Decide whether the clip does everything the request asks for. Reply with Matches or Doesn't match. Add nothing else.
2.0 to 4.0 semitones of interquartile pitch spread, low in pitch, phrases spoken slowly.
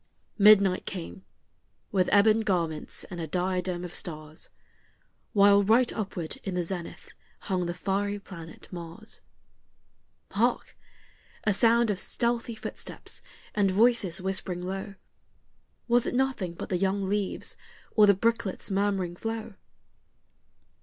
Doesn't match